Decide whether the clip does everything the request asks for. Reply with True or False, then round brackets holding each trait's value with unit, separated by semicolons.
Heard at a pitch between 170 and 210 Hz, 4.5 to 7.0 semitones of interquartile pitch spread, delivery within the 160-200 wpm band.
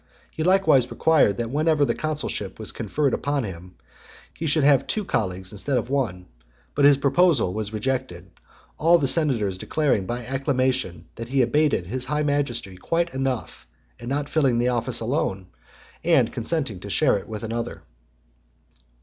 False (130 Hz; 5.2 semitones; 165 wpm)